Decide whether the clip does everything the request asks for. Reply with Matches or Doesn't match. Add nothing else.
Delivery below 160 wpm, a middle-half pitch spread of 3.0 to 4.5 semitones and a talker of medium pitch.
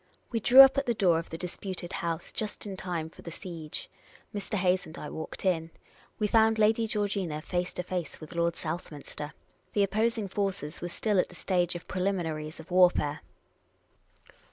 Doesn't match